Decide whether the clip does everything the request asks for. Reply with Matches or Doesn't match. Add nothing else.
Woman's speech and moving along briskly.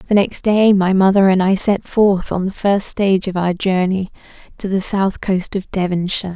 Matches